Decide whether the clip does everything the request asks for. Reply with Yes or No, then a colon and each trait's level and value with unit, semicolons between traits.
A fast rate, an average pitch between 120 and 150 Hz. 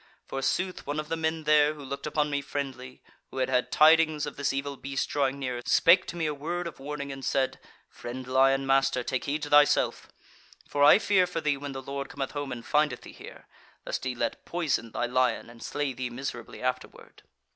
Yes: fast, 210 wpm; medium, 140 Hz